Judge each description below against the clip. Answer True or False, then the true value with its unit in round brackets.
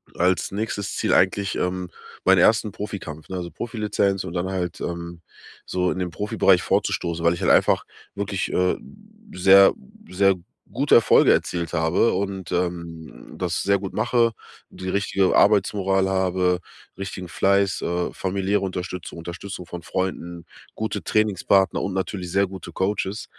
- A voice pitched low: True (95 Hz)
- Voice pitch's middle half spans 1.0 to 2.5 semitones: True (2.0 semitones)